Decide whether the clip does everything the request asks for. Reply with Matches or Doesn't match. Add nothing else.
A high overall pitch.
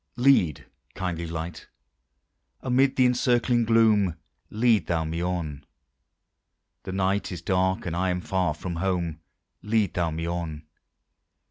Doesn't match